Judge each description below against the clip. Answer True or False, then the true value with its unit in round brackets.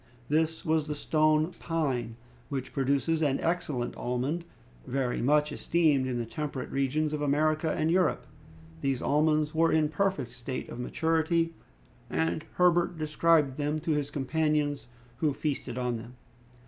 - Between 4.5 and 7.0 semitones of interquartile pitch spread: False (3.1 semitones)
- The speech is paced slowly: False (150 wpm)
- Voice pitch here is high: False (150 Hz)